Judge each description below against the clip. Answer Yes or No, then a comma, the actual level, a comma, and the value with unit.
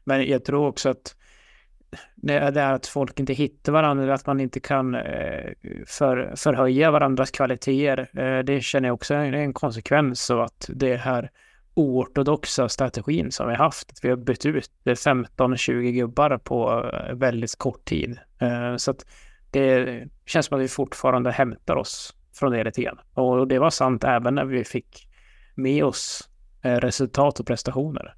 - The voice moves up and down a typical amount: No, narrow, 2.1 semitones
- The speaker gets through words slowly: No, average, 160 wpm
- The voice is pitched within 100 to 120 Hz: No, low, 130 Hz